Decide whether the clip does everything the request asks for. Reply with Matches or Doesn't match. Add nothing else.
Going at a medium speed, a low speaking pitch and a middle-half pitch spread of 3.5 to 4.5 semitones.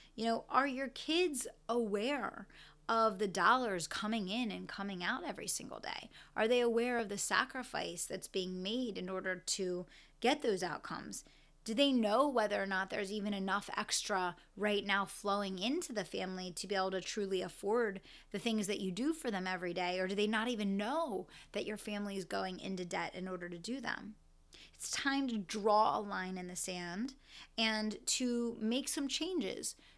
Doesn't match